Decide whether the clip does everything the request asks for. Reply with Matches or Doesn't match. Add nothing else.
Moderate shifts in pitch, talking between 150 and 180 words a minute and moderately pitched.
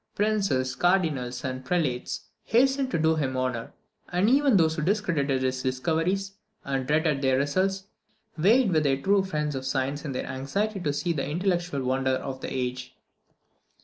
Doesn't match